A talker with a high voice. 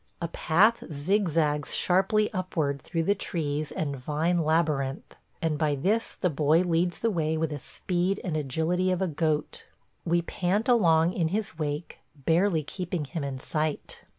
No: medium, 165 Hz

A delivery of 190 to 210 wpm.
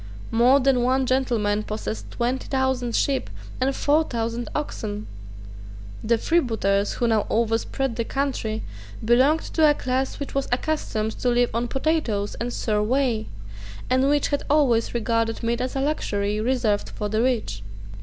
No: average, 155 wpm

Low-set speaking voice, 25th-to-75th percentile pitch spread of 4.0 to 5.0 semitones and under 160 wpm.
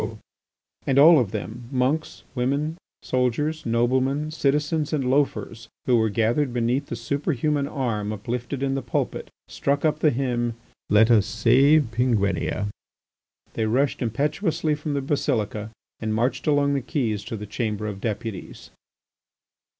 Yes: low, 125 Hz; average, 4.3 semitones; average, 140 wpm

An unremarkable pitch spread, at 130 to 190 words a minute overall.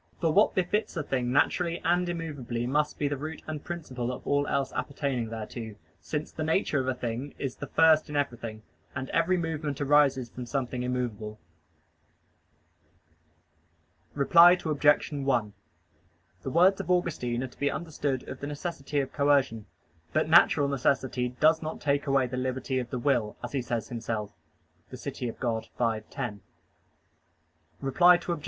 Yes: average, 4.0 semitones; average, 160 wpm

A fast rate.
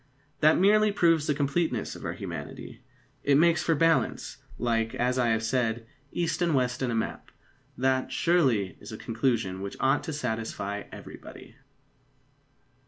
No: average, 155 wpm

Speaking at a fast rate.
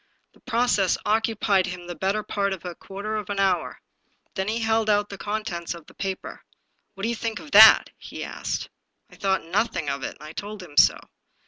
Yes: fast, 215 wpm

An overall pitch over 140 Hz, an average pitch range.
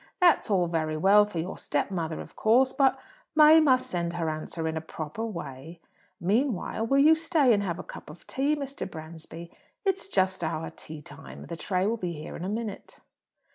No: medium, 185 Hz; wide, 7.8 semitones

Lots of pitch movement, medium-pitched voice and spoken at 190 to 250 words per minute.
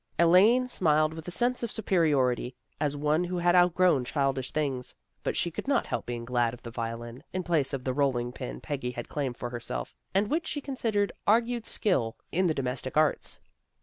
Yes: wide, 6.7 semitones; medium, 150 Hz; average, 195 wpm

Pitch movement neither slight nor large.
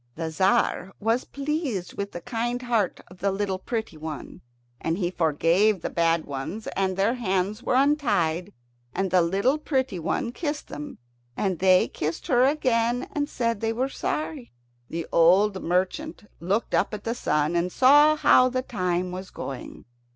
No: wide, 5.8 semitones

